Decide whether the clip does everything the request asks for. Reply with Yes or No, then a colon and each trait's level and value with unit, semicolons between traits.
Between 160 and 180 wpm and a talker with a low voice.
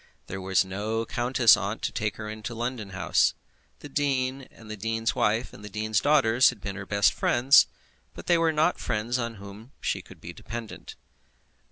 No: average, 195 wpm; low, 115 Hz